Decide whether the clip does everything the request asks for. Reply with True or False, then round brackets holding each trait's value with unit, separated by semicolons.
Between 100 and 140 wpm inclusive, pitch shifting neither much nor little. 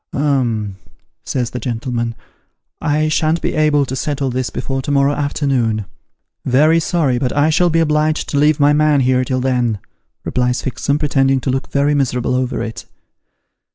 False (180 wpm; 3.0 semitones)